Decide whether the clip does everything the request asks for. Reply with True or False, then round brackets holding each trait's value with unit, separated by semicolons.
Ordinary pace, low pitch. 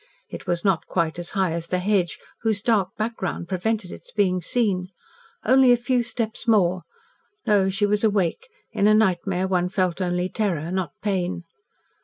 False (170 wpm; 190 Hz)